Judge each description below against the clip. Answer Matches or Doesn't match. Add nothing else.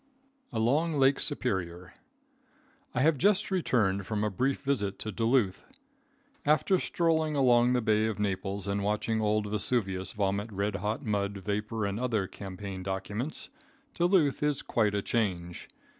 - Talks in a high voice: Doesn't match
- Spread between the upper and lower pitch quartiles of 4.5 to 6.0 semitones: Matches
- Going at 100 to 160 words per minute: Matches